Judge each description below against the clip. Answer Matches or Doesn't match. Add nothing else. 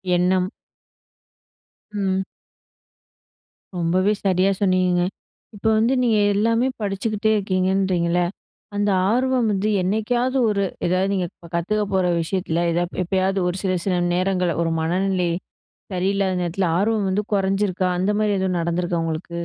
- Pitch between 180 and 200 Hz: Matches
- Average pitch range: Doesn't match